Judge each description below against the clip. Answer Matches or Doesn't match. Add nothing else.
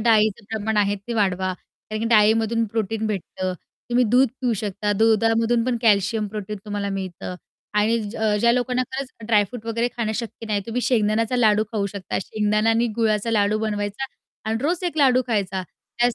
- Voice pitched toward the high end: Matches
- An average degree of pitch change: Doesn't match